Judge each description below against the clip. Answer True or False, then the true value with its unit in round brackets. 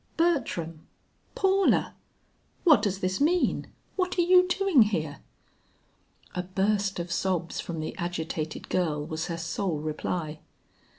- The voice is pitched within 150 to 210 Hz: True (185 Hz)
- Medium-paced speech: False (125 wpm)